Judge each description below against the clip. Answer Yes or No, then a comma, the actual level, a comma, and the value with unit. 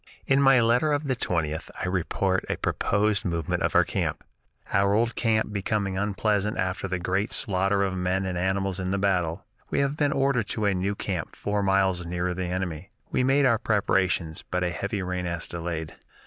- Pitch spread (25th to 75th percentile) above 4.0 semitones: No, average, 2.8 semitones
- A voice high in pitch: No, very low, 95 Hz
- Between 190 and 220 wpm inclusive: Yes, average, 195 wpm